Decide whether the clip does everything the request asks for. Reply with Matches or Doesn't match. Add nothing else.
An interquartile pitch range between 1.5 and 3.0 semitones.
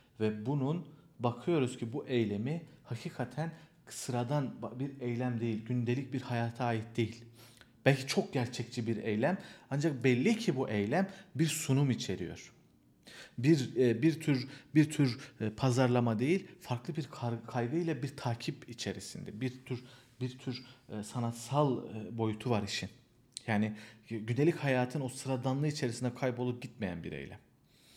Doesn't match